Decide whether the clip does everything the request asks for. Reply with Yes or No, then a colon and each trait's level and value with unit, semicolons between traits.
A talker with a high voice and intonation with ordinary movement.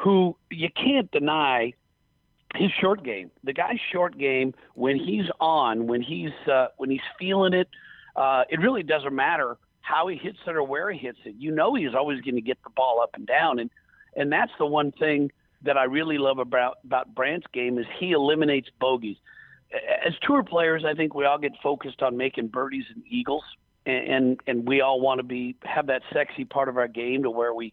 No: medium, 140 Hz; average, 4.5 semitones